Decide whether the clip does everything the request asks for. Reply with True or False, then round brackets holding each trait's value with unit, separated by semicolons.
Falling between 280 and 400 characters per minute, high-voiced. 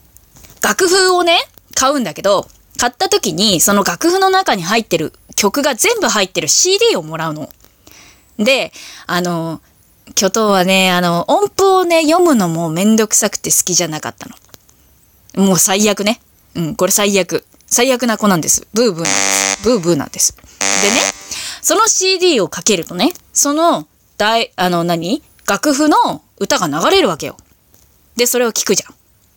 True (300 characters per minute; 210 Hz)